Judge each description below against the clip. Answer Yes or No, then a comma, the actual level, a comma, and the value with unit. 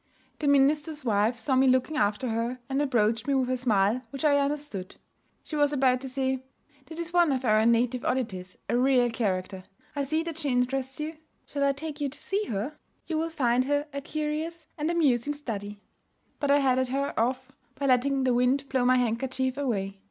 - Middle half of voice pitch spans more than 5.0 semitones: No, average, 3.2 semitones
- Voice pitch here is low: No, very high, 265 Hz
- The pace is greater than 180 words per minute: Yes, average, 200 wpm